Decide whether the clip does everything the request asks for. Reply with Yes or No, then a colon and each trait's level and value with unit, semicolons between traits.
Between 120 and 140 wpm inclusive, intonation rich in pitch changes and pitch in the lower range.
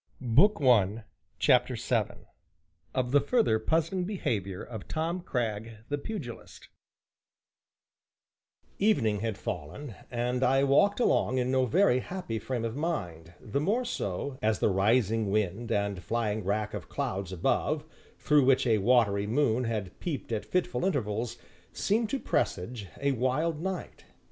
Yes: slow, 135 wpm; wide, 5.9 semitones; low, 125 Hz